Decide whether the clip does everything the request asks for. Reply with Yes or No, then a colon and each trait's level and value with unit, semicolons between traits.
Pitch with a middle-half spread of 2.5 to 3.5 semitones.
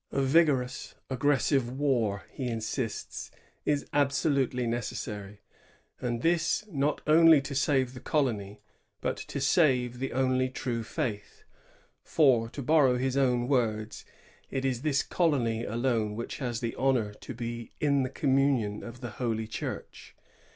Yes: average, 3.0 semitones